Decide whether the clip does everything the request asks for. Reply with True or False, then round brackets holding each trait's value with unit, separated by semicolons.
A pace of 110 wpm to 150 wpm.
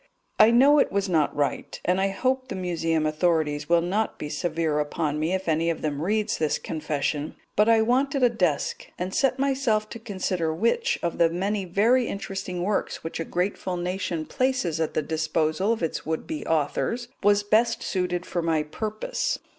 False (185 wpm)